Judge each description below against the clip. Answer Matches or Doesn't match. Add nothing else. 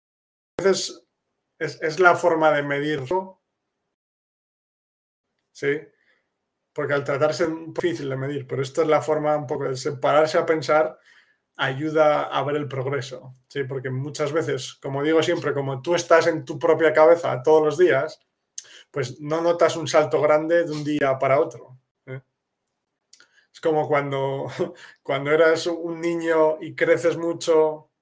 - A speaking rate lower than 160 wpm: Matches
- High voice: Doesn't match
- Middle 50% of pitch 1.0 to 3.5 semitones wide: Matches